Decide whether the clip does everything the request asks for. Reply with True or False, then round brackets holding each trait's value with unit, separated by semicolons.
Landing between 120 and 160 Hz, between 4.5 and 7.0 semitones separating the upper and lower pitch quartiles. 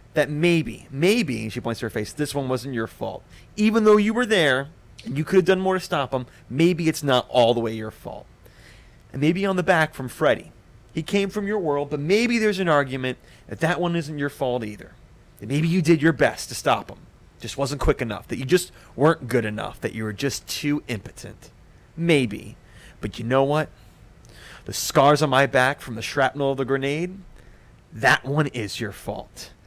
True (140 Hz; 5.5 semitones)